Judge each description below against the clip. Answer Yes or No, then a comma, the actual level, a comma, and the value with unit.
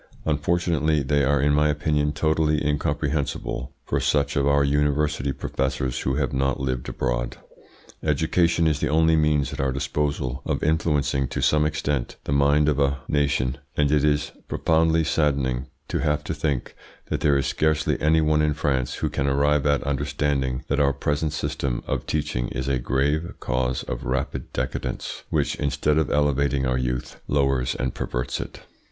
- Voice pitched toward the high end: No, very low, 70 Hz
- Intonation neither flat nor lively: No, narrow, 2.1 semitones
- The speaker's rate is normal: Yes, average, 170 wpm